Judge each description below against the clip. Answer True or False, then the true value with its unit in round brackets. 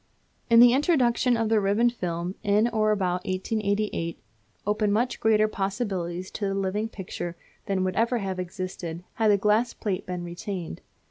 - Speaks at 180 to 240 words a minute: False (155 wpm)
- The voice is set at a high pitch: True (205 Hz)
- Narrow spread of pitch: False (3.2 semitones)